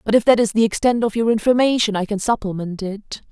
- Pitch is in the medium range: No, high, 215 Hz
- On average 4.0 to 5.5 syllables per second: No, 6.1 syllables/s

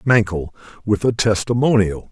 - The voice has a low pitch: Yes, low, 105 Hz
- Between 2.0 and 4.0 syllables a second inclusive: No, 4.7 syllables/s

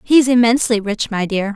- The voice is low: No, high, 225 Hz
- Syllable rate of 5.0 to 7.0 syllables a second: Yes, 5.5 syllables/s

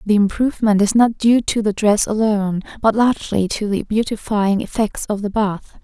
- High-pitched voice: Yes, high, 210 Hz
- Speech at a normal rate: Yes, average, 185 wpm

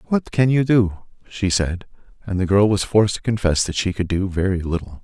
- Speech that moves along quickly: Yes, fast, 225 wpm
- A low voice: Yes, low, 100 Hz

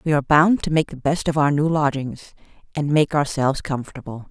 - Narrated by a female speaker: Yes, female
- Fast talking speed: Yes, fast, 210 wpm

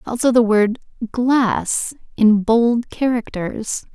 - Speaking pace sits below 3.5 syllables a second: Yes, 3.1 syllables/s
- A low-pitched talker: No, high, 230 Hz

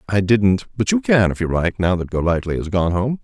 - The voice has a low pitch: Yes, low, 100 Hz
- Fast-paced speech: Yes, fast, 260 wpm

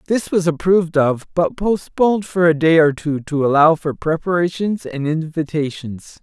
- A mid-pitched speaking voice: Yes, medium, 165 Hz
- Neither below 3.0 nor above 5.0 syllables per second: Yes, 4.7 syllables/s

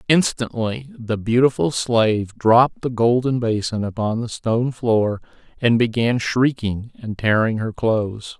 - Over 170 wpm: No, slow, 135 wpm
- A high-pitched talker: No, low, 115 Hz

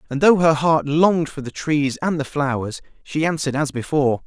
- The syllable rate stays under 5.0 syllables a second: No, 5.5 syllables/s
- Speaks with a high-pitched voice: No, medium, 150 Hz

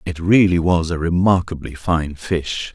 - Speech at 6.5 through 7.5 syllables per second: No, 4.2 syllables/s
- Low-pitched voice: Yes, very low, 85 Hz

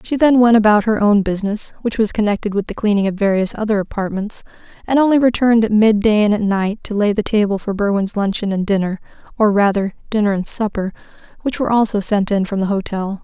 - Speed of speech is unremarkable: No, fast, 215 wpm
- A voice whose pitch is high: Yes, high, 210 Hz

